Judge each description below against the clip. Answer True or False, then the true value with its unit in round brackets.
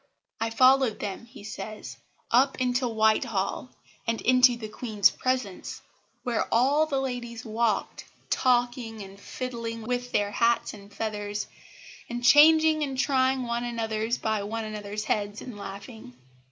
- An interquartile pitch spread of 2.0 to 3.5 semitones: True (2.9 semitones)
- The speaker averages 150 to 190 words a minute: False (140 wpm)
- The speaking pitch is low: False (235 Hz)